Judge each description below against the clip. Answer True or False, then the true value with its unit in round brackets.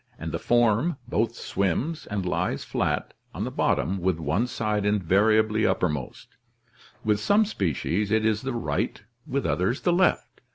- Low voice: True (105 Hz)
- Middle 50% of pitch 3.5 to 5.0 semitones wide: True (4.2 semitones)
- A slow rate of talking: False (165 wpm)